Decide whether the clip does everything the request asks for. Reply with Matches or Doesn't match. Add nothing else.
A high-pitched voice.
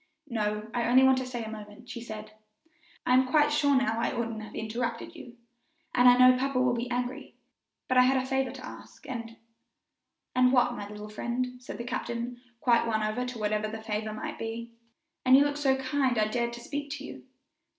Matches